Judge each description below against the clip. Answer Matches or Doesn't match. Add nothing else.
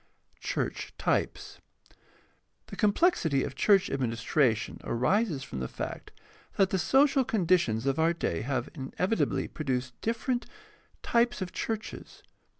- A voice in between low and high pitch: Matches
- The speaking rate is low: Matches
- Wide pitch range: Matches